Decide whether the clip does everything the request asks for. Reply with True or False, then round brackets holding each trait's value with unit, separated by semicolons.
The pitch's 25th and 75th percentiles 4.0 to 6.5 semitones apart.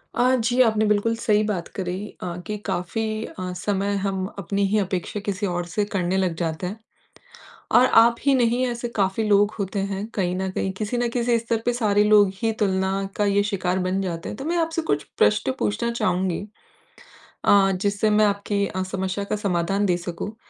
False (2.8 semitones)